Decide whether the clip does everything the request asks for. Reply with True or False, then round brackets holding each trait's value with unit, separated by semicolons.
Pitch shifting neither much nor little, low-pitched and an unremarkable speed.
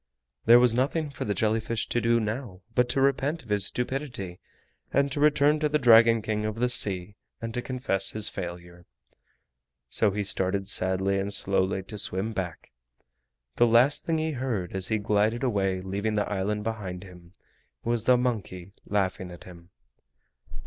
True (4.3 semitones; 105 Hz; 175 wpm)